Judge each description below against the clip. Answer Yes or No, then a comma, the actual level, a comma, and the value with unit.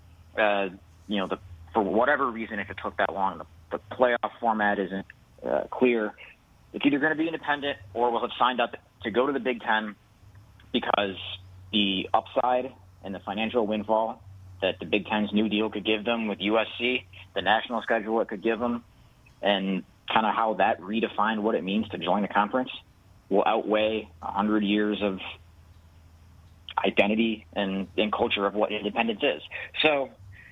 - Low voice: Yes, low, 105 Hz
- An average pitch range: Yes, average, 3.0 semitones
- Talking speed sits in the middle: Yes, average, 175 wpm